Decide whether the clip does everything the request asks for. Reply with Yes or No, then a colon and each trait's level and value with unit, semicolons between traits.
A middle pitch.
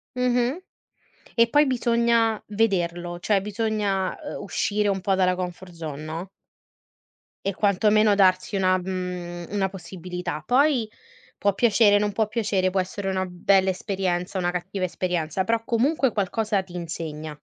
No: high, 195 Hz